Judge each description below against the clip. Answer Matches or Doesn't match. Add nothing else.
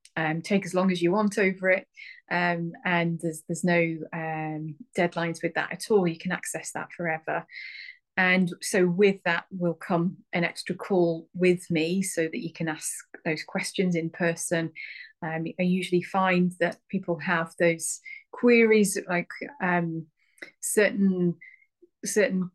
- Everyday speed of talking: Matches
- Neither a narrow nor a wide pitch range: Doesn't match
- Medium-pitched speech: Matches